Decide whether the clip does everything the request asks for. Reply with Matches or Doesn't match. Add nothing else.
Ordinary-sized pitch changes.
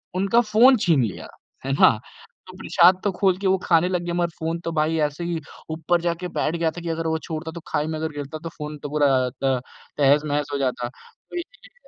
Matches